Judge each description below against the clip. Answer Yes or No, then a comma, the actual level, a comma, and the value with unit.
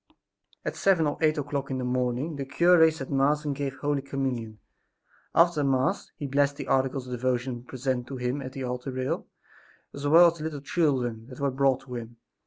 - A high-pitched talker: No, low, 135 Hz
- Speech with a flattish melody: Yes, narrow, 2.3 semitones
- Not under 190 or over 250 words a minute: Yes, average, 200 wpm